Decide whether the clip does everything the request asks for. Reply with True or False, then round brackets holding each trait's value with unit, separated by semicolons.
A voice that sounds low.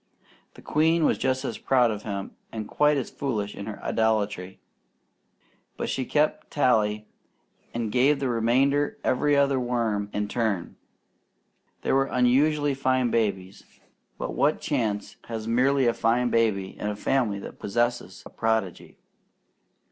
True (120 Hz)